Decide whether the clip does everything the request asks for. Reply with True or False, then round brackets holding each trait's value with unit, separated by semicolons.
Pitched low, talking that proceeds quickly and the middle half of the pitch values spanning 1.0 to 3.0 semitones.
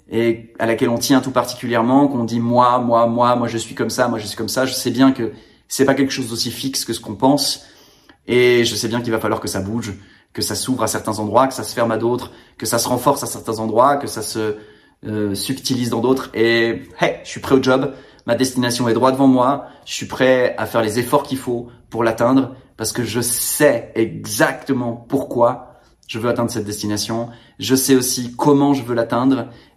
True (120 Hz; 230 wpm; 2.4 semitones)